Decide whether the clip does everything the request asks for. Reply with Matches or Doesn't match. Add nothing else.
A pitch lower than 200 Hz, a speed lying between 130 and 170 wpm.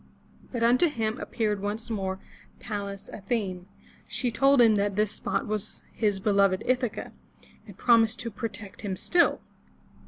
Doesn't match